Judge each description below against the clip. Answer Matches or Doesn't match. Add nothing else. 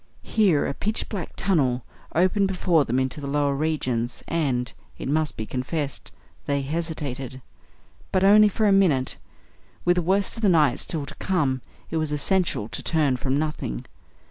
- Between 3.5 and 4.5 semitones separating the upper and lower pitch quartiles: Doesn't match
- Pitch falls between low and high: Matches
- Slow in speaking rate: Doesn't match